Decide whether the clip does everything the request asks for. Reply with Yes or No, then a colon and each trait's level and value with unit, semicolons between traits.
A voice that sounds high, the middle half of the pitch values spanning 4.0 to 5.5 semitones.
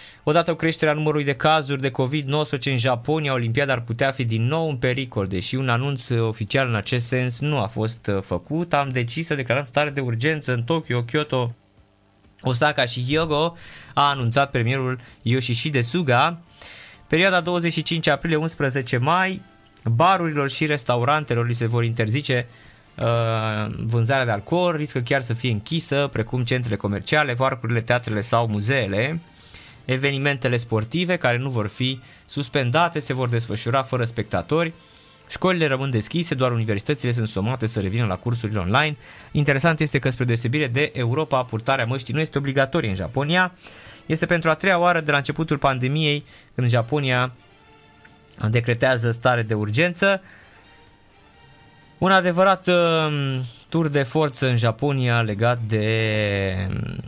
No: low, 130 Hz; average, 4.5 semitones